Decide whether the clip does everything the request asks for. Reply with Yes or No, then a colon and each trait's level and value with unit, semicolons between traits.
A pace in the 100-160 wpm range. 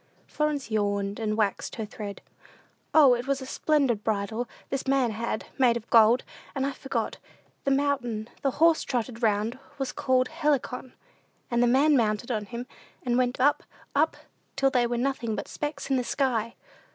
No: average, 175 wpm